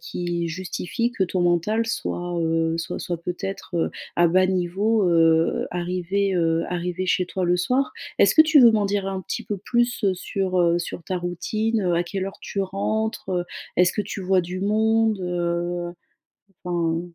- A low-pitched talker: No, medium, 180 Hz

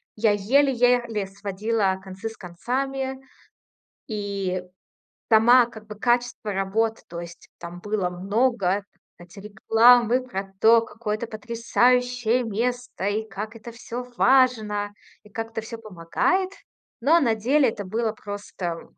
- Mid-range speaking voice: No, high, 220 Hz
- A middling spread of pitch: Yes, average, 3.3 semitones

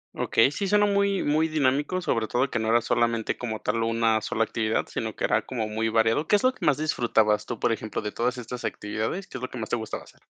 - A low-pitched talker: Yes, low, 120 Hz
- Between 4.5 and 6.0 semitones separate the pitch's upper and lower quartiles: Yes, average, 4.8 semitones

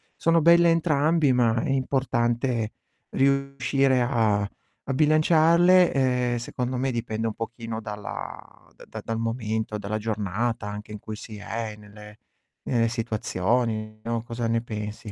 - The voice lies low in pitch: Yes, low, 115 Hz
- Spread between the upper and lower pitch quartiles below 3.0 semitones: No, average, 3.8 semitones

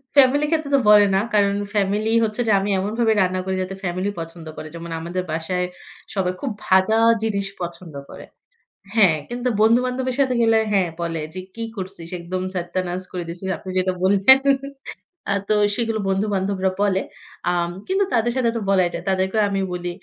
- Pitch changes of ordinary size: Yes, average, 3.5 semitones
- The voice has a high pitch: Yes, high, 195 Hz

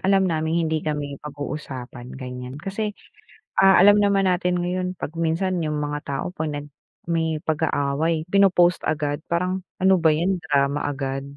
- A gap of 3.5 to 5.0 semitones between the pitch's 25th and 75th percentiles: Yes, average, 3.9 semitones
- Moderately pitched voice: Yes, medium, 160 Hz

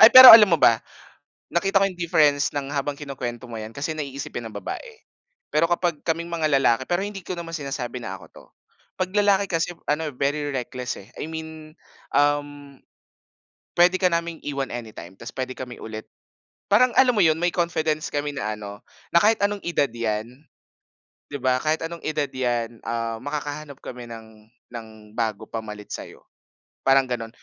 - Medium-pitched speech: Yes, medium, 145 Hz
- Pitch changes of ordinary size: No, wide, 5.8 semitones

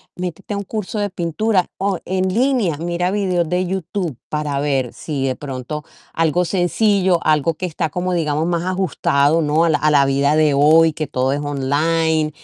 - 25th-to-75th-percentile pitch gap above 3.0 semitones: Yes, average, 3.8 semitones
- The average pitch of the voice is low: No, medium, 165 Hz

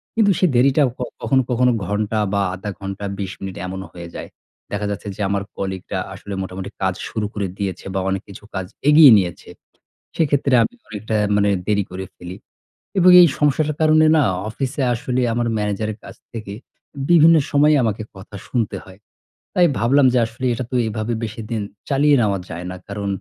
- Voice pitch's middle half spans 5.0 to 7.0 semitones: Yes, wide, 5.5 semitones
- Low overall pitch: Yes, low, 110 Hz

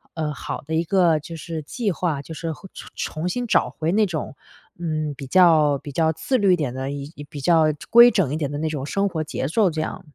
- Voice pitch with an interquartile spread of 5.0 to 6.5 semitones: No, average, 3.2 semitones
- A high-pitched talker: No, medium, 160 Hz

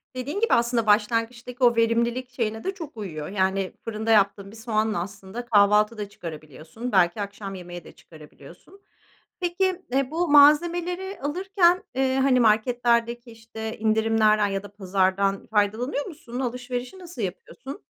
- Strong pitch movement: No, average, 4.4 semitones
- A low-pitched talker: No, high, 230 Hz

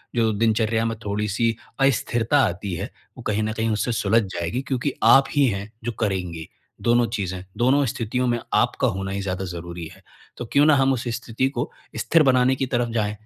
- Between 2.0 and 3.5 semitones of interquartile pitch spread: No, average, 3.9 semitones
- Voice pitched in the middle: No, low, 115 Hz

